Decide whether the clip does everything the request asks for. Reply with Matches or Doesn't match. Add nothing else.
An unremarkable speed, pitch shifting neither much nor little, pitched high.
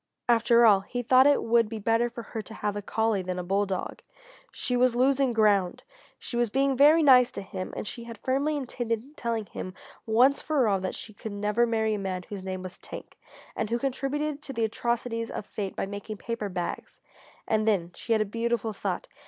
Doesn't match